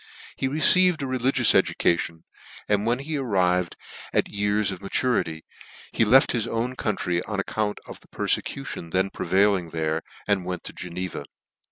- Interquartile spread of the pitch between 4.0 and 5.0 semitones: No, wide, 5.4 semitones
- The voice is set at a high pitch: No, low, 100 Hz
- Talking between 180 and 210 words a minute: No, average, 160 wpm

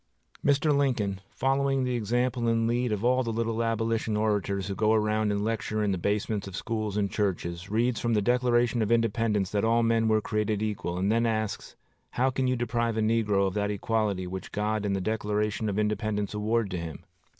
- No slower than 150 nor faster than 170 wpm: No, fast, 205 wpm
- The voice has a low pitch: Yes, low, 110 Hz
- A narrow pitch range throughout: Yes, narrow, 2.2 semitones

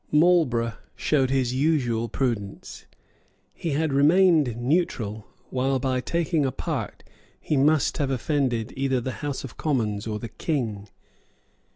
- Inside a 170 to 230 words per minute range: No, slow, 135 wpm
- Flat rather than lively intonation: No, average, 4.3 semitones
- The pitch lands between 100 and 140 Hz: Yes, low, 135 Hz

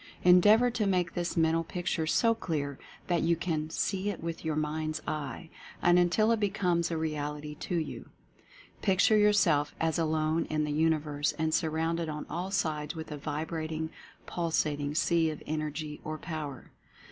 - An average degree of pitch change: No, narrow, 2.3 semitones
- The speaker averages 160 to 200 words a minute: Yes, average, 170 wpm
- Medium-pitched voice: Yes, medium, 160 Hz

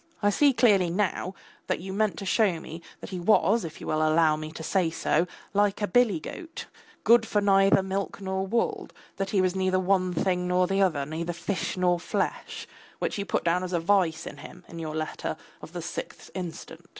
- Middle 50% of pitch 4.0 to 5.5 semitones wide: No, average, 2.9 semitones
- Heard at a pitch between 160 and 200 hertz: Yes, medium, 185 Hz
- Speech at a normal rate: No, fast, 210 wpm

